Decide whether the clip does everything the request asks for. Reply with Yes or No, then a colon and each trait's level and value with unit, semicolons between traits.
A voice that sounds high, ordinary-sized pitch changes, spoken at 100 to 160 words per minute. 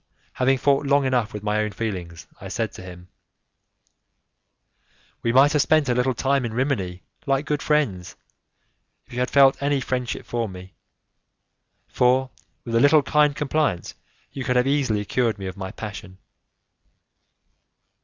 No: low, 125 Hz; average, 4.9 semitones; average, 155 wpm